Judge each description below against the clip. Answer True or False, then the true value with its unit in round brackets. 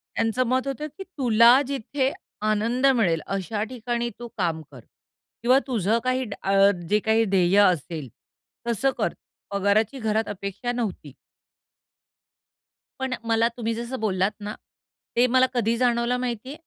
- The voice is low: False (230 Hz)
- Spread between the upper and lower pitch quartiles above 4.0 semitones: False (3.7 semitones)